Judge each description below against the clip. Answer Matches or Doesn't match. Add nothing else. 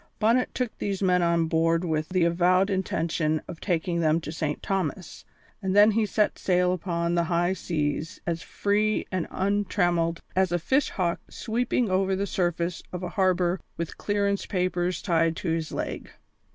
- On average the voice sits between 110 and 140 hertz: Doesn't match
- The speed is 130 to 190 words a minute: Matches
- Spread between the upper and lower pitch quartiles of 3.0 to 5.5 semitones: Doesn't match